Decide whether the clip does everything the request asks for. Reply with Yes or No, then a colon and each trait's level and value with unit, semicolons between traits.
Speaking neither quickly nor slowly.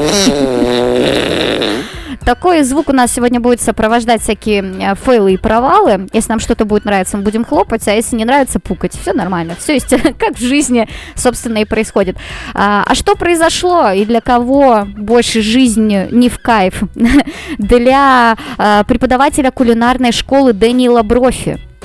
Yes: average, 140 wpm